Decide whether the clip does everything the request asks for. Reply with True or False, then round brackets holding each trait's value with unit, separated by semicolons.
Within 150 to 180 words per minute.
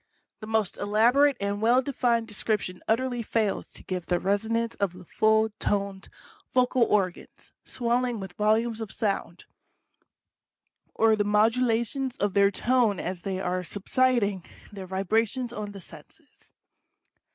False (140 wpm)